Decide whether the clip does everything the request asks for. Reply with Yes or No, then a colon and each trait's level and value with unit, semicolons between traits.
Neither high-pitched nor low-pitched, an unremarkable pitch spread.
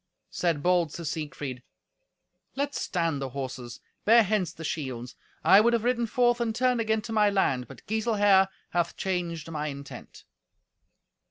No: medium, 180 Hz; wide, 6.9 semitones